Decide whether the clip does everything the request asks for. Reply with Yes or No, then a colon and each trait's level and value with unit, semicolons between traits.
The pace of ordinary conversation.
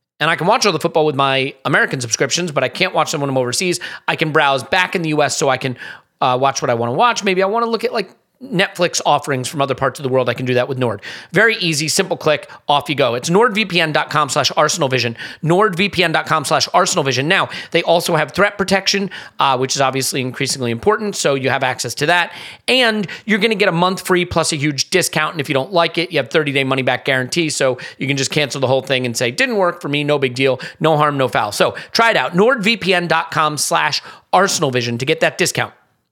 No: fast, 240 wpm